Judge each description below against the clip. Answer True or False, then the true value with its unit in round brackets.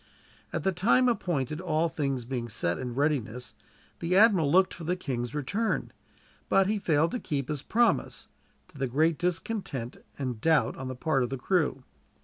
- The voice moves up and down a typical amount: False (5.7 semitones)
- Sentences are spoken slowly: False (175 wpm)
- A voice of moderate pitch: True (150 Hz)